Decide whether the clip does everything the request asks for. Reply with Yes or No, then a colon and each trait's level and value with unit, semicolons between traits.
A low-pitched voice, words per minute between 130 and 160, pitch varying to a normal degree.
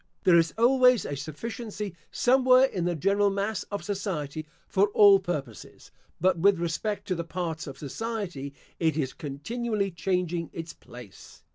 No: medium, 180 Hz; average, 150 wpm; average, 4.7 semitones